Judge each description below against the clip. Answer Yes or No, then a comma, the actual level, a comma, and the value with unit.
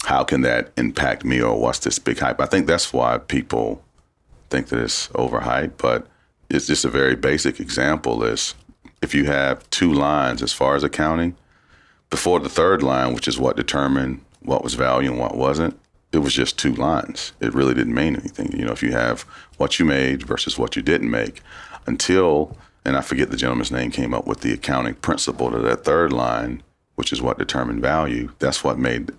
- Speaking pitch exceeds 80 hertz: No, very low, 65 Hz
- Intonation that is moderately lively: No, narrow, 2.0 semitones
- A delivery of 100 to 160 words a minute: No, average, 200 wpm